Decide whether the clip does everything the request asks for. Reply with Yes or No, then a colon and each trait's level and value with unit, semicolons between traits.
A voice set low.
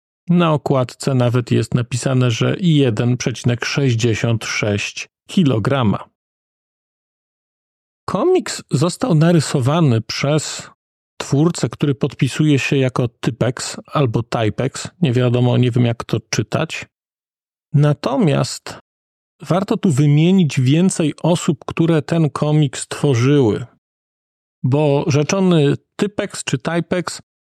No: medium, 145 Hz